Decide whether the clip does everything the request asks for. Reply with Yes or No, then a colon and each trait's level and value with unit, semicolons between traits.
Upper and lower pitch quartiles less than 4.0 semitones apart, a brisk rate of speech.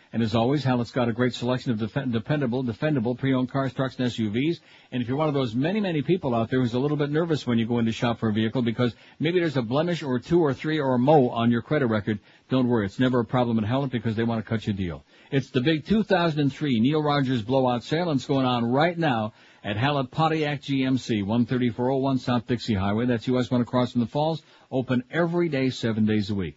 Yes: average, 3.4 semitones; fast, 245 wpm